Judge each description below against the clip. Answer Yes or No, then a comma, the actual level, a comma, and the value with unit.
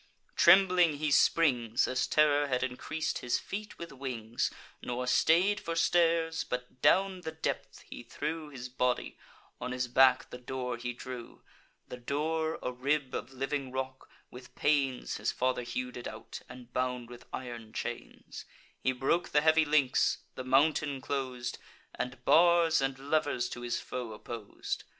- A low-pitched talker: Yes, low, 130 Hz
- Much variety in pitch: No, average, 3.7 semitones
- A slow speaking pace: No, average, 155 wpm